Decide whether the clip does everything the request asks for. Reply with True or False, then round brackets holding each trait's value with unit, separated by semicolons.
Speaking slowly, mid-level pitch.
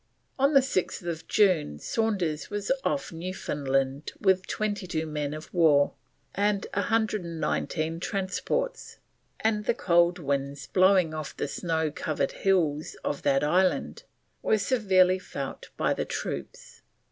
True (125 wpm; 175 Hz)